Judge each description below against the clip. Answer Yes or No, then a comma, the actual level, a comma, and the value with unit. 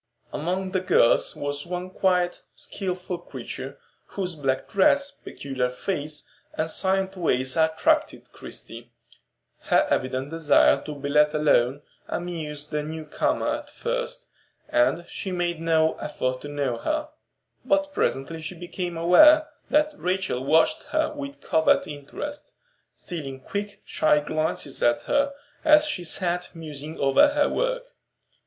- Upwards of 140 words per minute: No, slow, 135 wpm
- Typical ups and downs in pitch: No, wide, 5.9 semitones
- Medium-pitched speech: Yes, medium, 170 Hz